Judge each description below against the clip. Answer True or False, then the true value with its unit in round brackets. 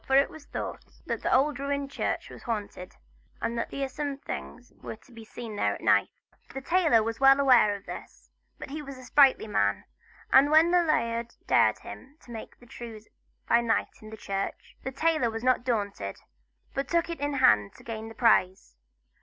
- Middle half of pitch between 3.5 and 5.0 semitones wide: True (4.0 semitones)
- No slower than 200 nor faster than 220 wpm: True (205 wpm)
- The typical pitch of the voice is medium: False (245 Hz)